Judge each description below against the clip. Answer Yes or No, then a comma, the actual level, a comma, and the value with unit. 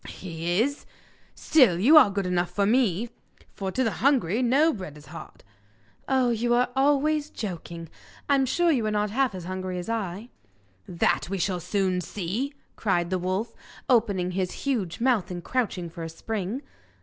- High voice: Yes, high, 205 Hz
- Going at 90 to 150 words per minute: No, average, 175 wpm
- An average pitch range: No, wide, 5.9 semitones